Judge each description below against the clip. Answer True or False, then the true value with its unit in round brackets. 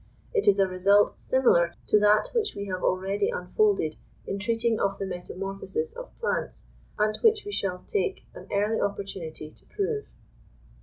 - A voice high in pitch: True (205 Hz)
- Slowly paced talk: False (160 wpm)